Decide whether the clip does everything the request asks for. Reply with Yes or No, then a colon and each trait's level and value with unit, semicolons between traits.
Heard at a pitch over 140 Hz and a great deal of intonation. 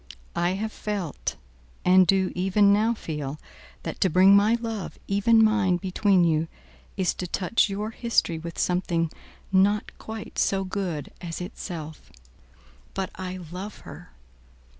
No: high, 190 Hz; average, 2.9 semitones